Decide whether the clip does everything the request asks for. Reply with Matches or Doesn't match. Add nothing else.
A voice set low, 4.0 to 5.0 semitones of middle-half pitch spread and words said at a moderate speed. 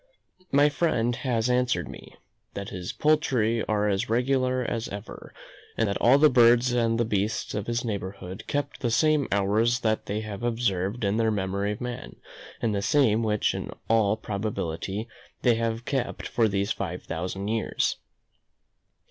Doesn't match